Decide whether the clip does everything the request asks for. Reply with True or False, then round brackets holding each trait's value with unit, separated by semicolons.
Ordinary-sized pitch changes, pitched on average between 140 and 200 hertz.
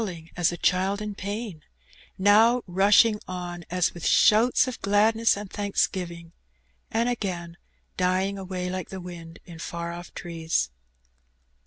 True (3.1 semitones; 185 Hz)